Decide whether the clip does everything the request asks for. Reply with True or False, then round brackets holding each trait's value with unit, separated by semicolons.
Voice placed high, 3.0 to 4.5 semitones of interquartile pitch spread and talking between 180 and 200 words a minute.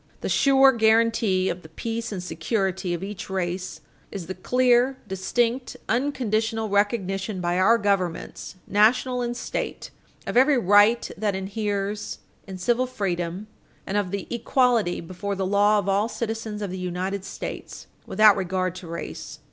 False (205 Hz; 3.5 semitones; 150 wpm)